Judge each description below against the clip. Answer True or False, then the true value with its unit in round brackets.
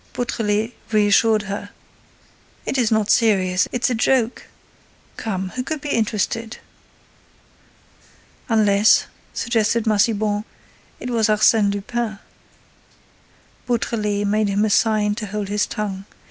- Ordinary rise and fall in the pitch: False (1.9 semitones)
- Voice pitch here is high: True (215 Hz)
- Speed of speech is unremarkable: False (110 wpm)